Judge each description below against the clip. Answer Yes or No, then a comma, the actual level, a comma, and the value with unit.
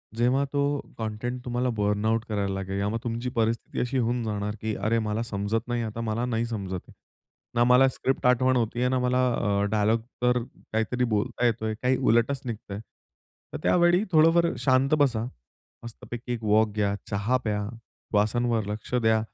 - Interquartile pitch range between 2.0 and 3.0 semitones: Yes, average, 2.7 semitones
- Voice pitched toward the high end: No, low, 115 Hz